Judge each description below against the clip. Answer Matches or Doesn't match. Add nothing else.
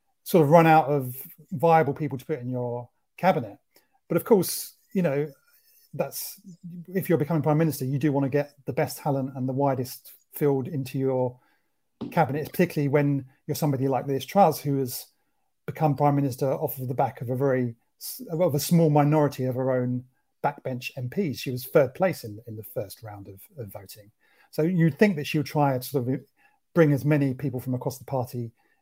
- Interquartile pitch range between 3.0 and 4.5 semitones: Matches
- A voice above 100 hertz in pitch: Matches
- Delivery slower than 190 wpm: Doesn't match